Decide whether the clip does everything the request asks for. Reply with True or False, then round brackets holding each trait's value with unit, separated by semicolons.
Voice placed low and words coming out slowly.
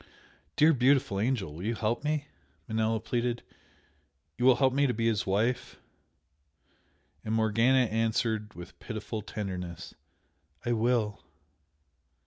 True (115 Hz; 120 wpm)